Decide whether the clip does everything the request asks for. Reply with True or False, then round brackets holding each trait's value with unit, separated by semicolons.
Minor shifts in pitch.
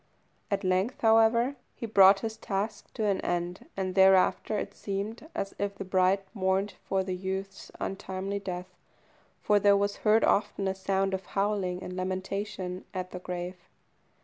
True (1.6 semitones)